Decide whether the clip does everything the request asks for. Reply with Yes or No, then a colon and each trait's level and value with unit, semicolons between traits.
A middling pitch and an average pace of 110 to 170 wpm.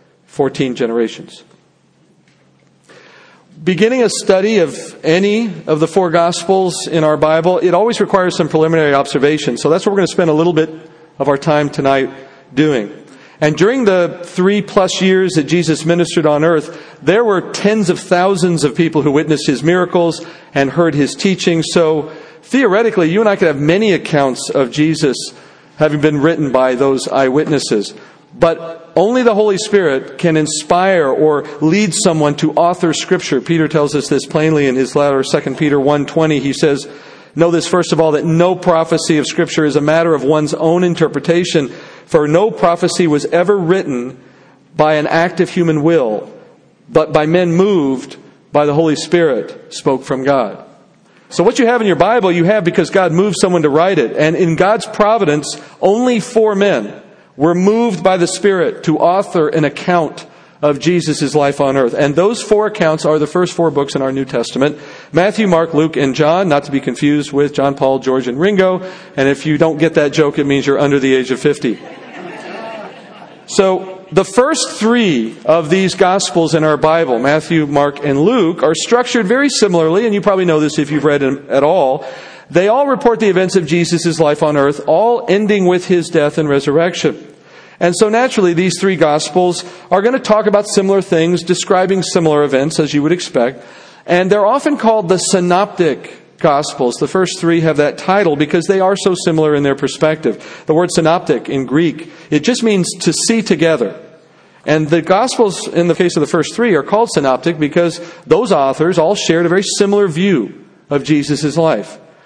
No: medium, 165 Hz; average, 185 wpm